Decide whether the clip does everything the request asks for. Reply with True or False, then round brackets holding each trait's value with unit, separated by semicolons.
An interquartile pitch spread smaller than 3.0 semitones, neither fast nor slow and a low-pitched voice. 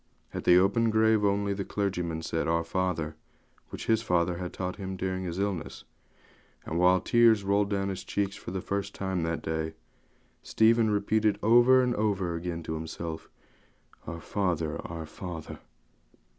False (3.4 semitones; 165 wpm; 95 Hz)